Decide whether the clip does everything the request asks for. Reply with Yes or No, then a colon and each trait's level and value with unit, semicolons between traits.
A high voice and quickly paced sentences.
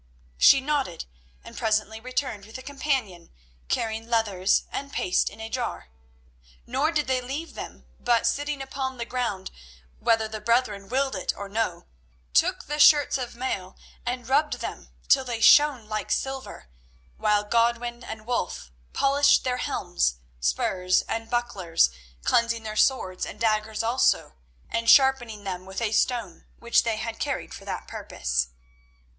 No: high, 230 Hz; average, 150 wpm